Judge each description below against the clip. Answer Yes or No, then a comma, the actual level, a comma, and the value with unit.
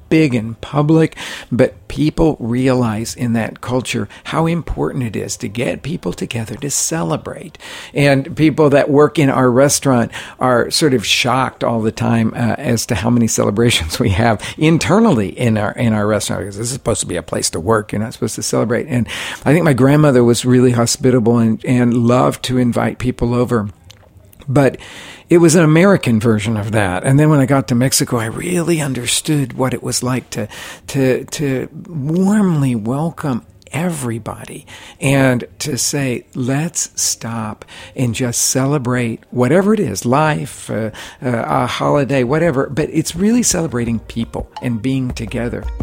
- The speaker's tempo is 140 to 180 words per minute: Yes, average, 170 wpm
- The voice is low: Yes, low, 125 Hz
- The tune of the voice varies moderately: Yes, average, 4.0 semitones